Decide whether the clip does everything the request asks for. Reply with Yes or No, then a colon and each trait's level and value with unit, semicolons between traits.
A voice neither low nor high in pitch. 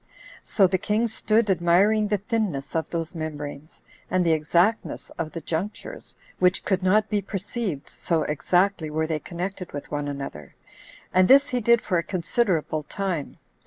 Yes: medium, 180 Hz